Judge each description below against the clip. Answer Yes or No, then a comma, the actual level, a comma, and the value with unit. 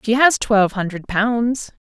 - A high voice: Yes, high, 220 Hz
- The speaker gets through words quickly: No, average, 160 wpm